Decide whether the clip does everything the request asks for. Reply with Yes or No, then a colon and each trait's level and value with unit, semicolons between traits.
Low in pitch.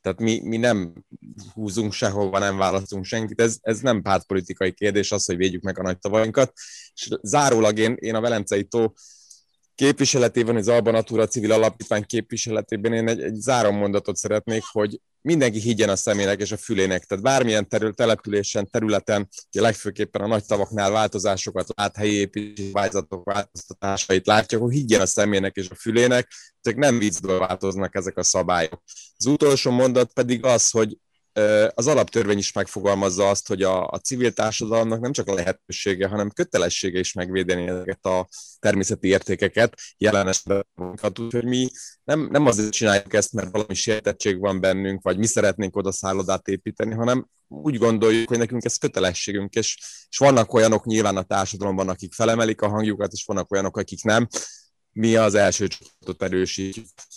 Yes: low, 105 Hz